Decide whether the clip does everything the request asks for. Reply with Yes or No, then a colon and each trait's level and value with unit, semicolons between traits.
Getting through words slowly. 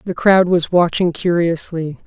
No: average, 145 wpm